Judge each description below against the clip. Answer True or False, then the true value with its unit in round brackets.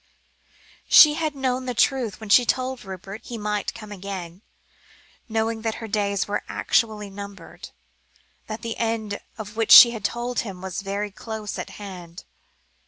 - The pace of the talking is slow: False (160 wpm)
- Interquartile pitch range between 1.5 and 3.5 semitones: True (2.4 semitones)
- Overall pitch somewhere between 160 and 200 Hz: False (215 Hz)